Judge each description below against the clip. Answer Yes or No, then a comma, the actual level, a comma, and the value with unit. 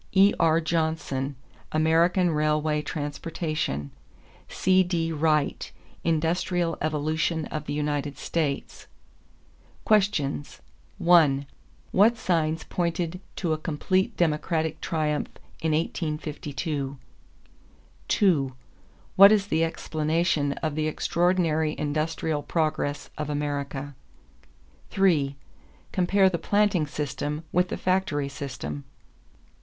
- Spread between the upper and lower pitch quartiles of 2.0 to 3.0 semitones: Yes, average, 2.7 semitones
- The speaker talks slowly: Yes, slow, 95 wpm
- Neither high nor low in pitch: Yes, medium, 155 Hz